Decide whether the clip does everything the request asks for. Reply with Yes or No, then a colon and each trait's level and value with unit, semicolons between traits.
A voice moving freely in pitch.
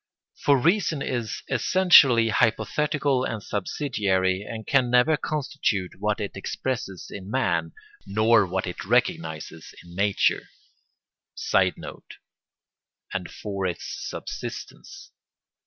Yes: wide, 6.1 semitones